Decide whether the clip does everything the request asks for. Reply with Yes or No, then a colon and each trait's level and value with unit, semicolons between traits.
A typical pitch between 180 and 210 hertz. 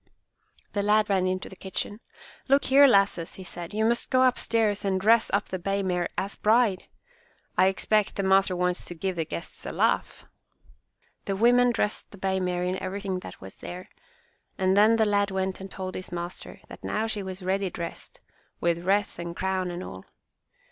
Yes: high, 190 Hz